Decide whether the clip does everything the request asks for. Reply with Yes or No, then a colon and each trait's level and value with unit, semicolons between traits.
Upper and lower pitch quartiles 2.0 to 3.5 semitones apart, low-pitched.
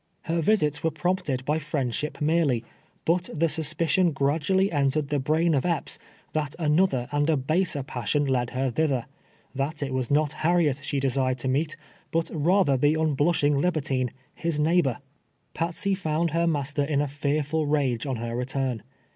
No: average, 3.2 semitones; medium, 150 Hz